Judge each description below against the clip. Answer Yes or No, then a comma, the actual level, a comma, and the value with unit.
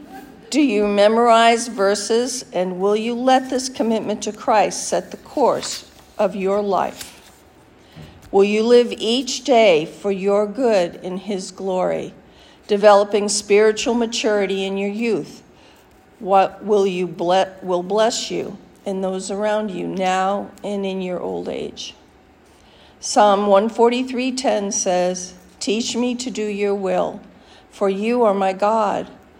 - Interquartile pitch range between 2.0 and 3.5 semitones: Yes, average, 3.1 semitones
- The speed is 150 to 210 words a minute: No, slow, 135 wpm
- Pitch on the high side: Yes, high, 205 Hz